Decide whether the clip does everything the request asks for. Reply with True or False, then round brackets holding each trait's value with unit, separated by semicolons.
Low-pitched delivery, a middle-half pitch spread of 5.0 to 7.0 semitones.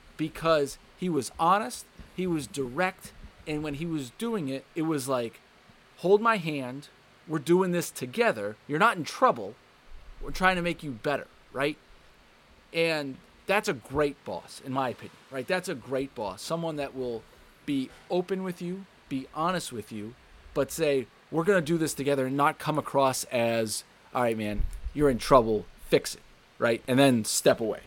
False (145 Hz; 5.3 semitones)